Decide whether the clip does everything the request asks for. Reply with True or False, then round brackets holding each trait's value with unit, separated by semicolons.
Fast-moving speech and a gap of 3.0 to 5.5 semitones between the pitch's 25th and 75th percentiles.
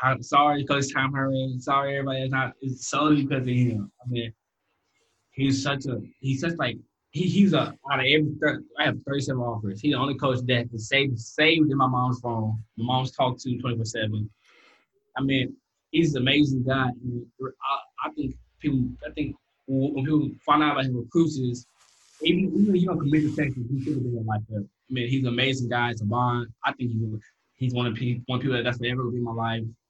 False (220 wpm; 2.6 semitones)